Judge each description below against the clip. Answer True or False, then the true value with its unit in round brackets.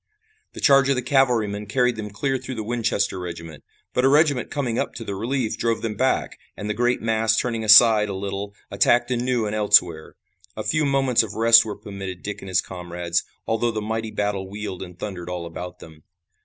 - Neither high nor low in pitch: False (110 Hz)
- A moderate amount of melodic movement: True (3.8 semitones)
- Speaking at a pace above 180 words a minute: True (205 wpm)